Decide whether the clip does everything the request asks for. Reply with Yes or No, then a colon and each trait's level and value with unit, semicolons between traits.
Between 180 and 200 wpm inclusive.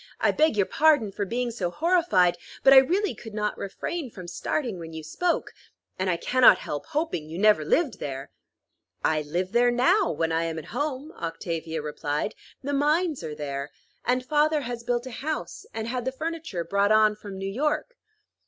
Yes: average, 190 wpm